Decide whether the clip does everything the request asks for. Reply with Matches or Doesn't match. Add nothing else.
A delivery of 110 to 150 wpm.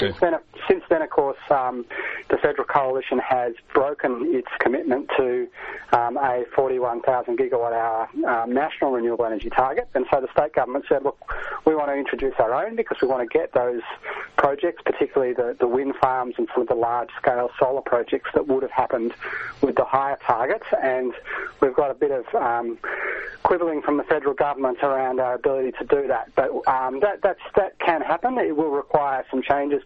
Doesn't match